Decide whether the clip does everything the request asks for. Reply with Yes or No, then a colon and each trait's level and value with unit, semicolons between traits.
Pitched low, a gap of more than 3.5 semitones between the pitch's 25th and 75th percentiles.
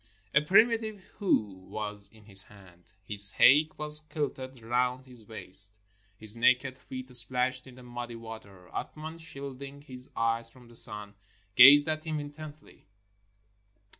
Yes: low, 125 Hz; average, 5.0 semitones